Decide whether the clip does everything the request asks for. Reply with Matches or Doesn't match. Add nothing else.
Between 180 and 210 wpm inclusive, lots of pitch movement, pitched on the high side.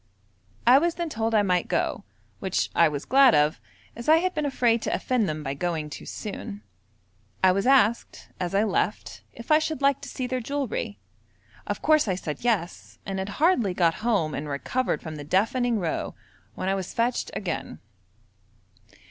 Matches